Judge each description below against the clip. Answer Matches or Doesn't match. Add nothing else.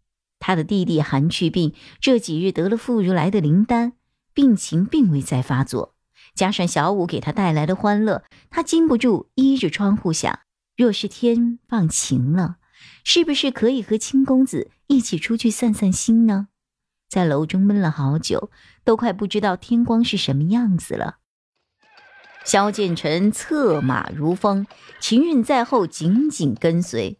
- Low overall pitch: Doesn't match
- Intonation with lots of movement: Matches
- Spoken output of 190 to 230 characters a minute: Matches